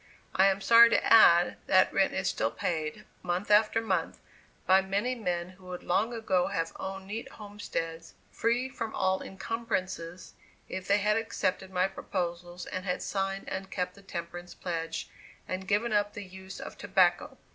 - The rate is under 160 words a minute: No, average, 170 wpm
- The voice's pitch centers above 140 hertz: Yes, high, 190 Hz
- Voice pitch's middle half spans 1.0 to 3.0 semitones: Yes, narrow, 2.5 semitones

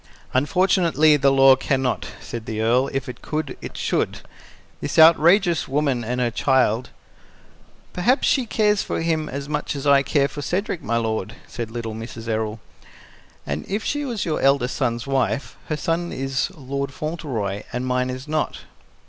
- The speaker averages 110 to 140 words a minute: No, average, 175 wpm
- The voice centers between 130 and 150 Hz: Yes, low, 135 Hz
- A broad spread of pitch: No, average, 4.4 semitones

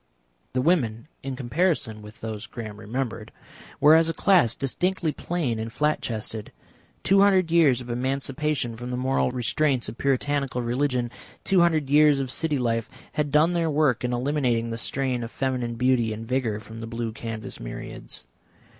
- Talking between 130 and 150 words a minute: No, average, 170 wpm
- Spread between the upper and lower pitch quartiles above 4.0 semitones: Yes, average, 4.6 semitones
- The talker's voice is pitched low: Yes, low, 130 Hz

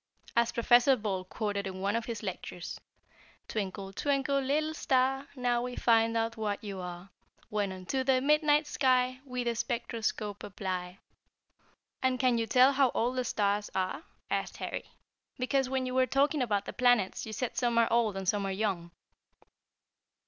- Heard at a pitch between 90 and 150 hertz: No, high, 235 Hz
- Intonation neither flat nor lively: Yes, average, 4.2 semitones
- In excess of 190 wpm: No, average, 170 wpm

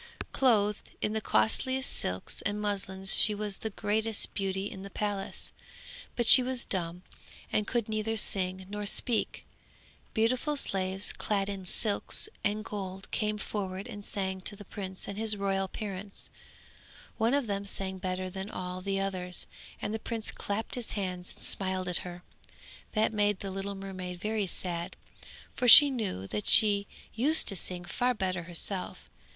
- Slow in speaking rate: No, average, 165 wpm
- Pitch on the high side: Yes, high, 200 Hz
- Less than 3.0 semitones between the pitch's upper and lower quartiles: Yes, narrow, 2.4 semitones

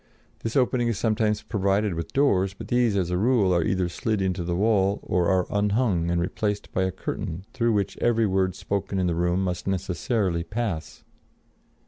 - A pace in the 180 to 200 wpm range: Yes, average, 185 wpm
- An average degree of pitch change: Yes, average, 3.4 semitones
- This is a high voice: No, very low, 95 Hz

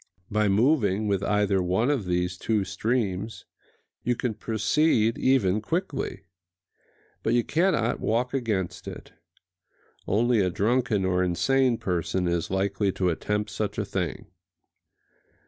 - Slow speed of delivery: Yes, slow, 130 wpm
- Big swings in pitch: No, average, 4.2 semitones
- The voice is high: No, low, 105 Hz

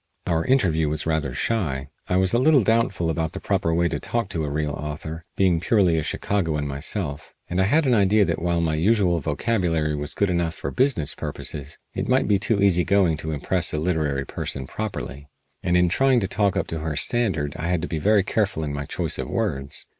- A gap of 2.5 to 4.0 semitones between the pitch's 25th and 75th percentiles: No, average, 4.7 semitones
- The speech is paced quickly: Yes, fast, 220 wpm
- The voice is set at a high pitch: No, very low, 85 Hz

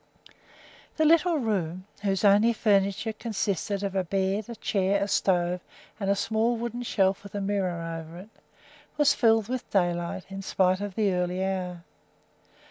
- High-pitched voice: Yes, high, 195 Hz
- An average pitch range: Yes, average, 3.0 semitones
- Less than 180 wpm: Yes, average, 160 wpm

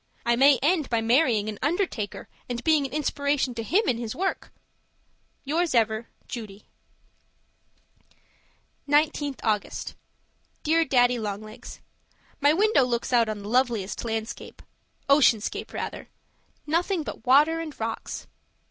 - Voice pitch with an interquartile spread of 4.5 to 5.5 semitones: Yes, average, 5.1 semitones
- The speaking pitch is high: Yes, very high, 255 Hz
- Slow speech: Yes, slow, 130 wpm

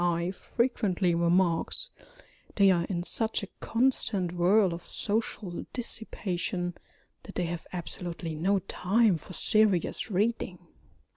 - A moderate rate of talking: No, slow, 120 wpm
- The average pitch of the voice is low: No, medium, 185 Hz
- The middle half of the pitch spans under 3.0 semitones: No, average, 3.7 semitones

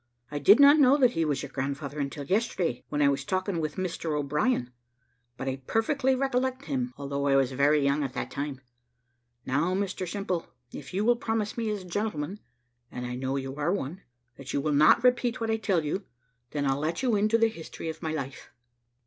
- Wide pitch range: Yes, wide, 7.9 semitones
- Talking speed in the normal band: No, fast, 210 wpm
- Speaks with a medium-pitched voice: Yes, medium, 165 Hz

